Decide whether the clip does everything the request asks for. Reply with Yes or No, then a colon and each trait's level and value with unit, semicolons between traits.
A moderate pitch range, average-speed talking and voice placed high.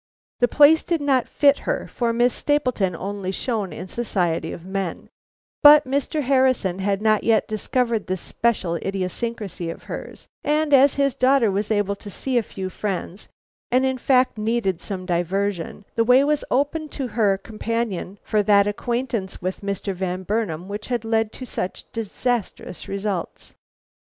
Yes: average, 4.7 semitones; average, 165 wpm; high, 215 Hz